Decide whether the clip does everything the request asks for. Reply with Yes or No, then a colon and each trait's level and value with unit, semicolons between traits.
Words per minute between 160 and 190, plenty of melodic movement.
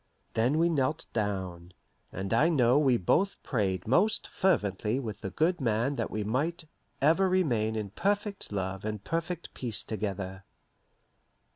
No: average, 145 wpm; wide, 8.2 semitones